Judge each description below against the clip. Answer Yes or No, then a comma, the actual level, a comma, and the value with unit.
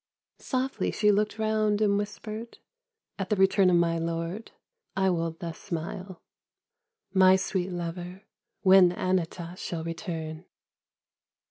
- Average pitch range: Yes, average, 3.6 semitones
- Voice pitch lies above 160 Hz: Yes, medium, 185 Hz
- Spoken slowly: Yes, slow, 125 wpm